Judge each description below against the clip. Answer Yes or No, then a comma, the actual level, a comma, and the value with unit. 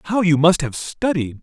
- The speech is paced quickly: Yes, fast, 210 wpm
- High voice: No, medium, 165 Hz